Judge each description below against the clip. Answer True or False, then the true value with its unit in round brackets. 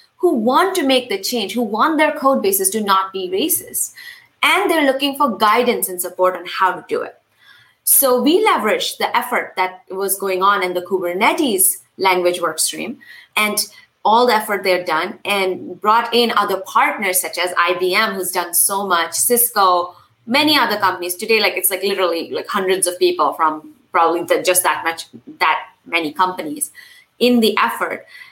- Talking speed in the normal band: True (180 wpm)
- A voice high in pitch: True (195 Hz)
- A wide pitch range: True (6.0 semitones)